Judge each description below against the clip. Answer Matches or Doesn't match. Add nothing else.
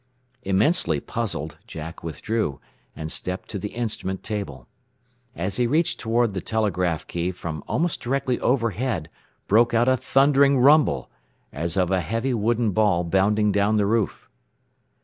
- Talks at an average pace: Matches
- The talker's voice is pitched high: Doesn't match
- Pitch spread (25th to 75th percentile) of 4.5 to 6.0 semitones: Matches